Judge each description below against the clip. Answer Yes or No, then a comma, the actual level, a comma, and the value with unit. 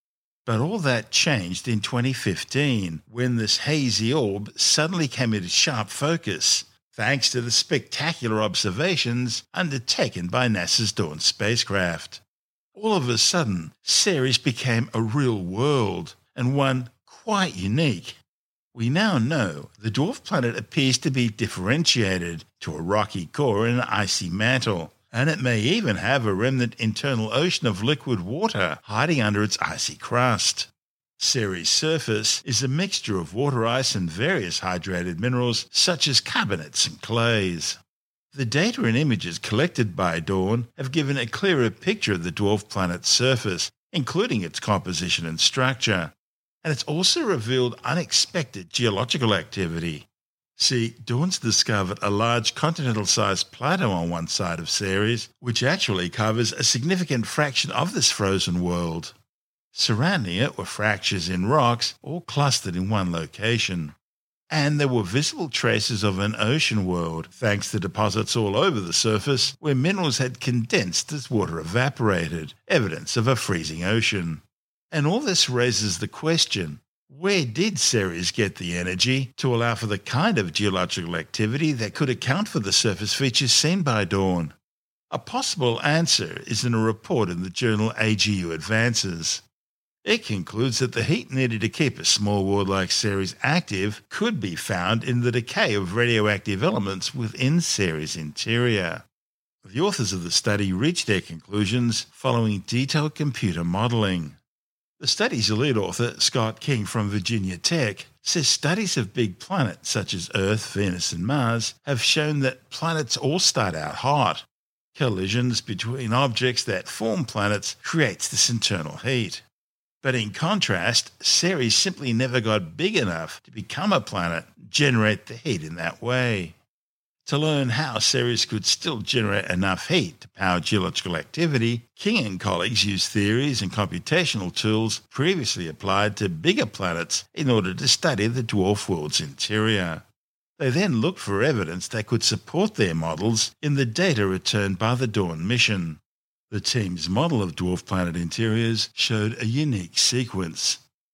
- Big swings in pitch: No, average, 5.0 semitones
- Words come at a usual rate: Yes, average, 150 wpm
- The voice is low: Yes, low, 115 Hz